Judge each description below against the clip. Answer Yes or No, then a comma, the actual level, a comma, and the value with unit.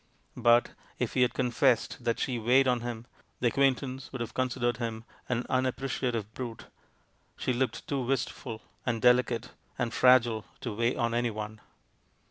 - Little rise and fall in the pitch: Yes, narrow, 1.8 semitones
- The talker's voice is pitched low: Yes, low, 120 Hz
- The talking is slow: No, average, 155 wpm